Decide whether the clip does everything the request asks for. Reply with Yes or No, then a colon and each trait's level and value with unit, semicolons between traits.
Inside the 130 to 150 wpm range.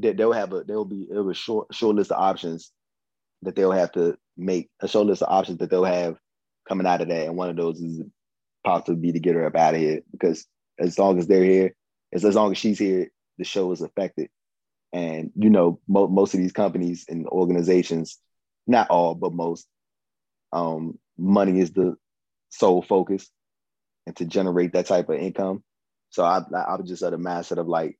No: average, 200 wpm